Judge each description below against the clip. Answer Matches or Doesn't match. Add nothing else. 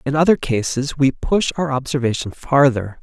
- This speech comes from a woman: Doesn't match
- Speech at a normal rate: Matches